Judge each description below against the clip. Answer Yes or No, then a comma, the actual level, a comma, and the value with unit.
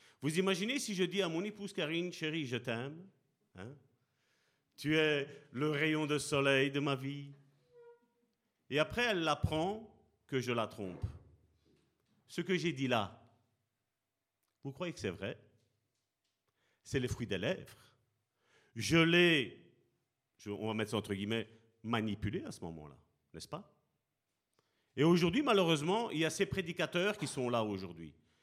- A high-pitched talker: No, medium, 140 Hz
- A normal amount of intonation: No, wide, 7.1 semitones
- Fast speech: No, average, 150 wpm